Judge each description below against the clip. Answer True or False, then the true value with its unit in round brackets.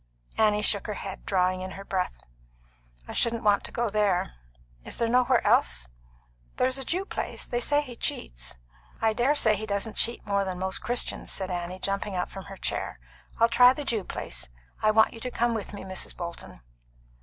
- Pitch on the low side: False (210 Hz)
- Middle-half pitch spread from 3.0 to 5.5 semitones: True (3.9 semitones)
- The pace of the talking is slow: False (195 wpm)